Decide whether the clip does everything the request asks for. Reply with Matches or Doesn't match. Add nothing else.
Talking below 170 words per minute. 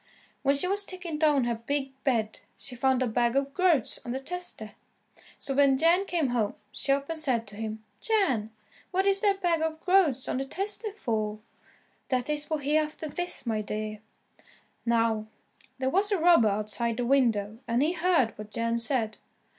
Doesn't match